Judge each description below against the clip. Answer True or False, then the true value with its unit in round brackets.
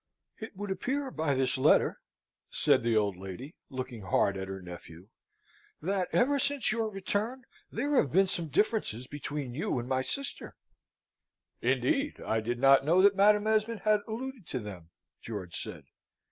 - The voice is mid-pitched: True (155 Hz)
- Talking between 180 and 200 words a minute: False (160 wpm)